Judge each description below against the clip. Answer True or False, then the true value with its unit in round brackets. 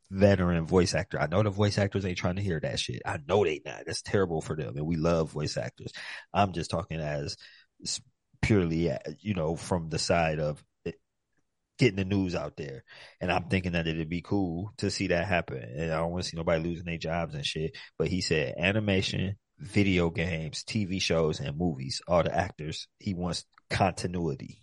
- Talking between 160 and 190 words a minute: False (200 wpm)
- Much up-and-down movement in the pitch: False (3.3 semitones)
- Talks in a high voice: False (90 Hz)